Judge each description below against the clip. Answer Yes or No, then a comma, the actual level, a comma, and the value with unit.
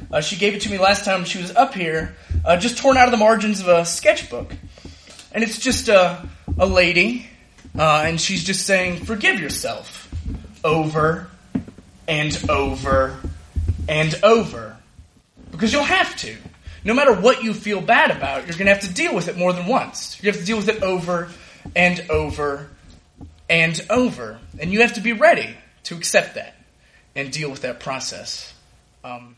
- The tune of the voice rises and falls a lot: Yes, wide, 7.3 semitones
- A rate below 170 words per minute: No, average, 180 wpm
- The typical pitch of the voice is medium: Yes, medium, 175 Hz